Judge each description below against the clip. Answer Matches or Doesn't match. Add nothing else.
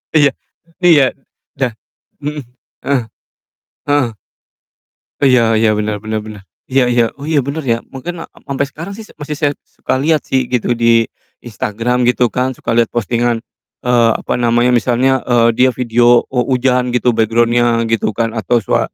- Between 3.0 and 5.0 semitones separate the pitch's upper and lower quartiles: Doesn't match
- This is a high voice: Doesn't match